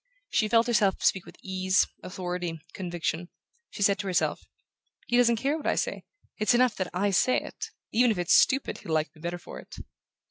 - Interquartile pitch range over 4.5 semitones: Yes, average, 4.9 semitones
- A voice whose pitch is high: Yes, high, 195 Hz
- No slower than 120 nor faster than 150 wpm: No, average, 200 wpm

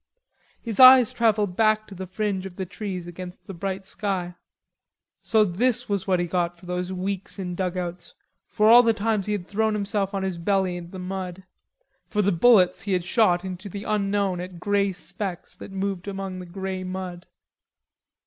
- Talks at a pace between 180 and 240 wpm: Yes, average, 185 wpm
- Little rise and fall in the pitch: Yes, narrow, 2.2 semitones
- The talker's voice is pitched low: No, high, 190 Hz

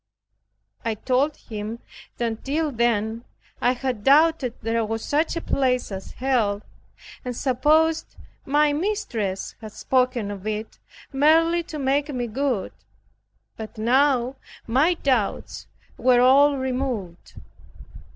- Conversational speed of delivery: No, slow, 120 wpm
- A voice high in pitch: Yes, very high, 255 Hz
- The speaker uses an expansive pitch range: No, average, 4.3 semitones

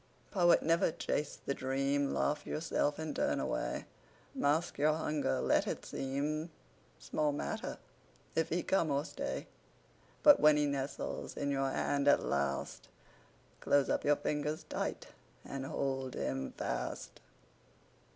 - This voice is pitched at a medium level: Yes, medium, 145 Hz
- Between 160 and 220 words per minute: No, slow, 135 wpm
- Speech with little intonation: Yes, narrow, 2.1 semitones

